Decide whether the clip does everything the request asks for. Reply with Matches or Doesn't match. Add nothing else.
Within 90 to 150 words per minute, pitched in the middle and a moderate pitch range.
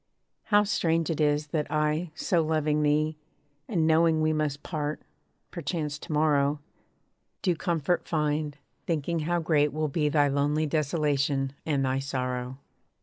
Doesn't match